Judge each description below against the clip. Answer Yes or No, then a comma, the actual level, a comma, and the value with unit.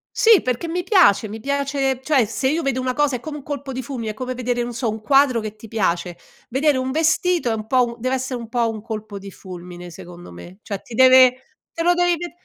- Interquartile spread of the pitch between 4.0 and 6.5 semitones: Yes, average, 4.4 semitones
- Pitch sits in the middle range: No, very high, 255 Hz